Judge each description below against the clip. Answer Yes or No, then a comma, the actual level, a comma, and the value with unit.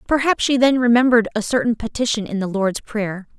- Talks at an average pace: Yes, average, 195 wpm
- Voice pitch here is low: No, high, 230 Hz